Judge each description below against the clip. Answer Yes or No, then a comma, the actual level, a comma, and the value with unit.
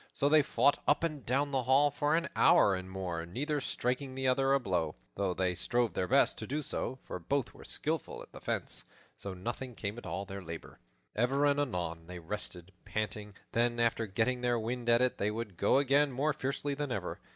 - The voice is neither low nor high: No, low, 120 Hz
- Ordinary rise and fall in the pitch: No, wide, 6.1 semitones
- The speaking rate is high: Yes, fast, 215 wpm